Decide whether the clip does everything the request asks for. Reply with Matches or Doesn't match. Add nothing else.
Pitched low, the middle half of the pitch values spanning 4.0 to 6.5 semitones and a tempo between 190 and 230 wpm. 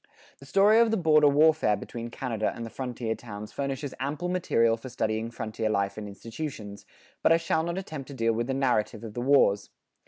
Matches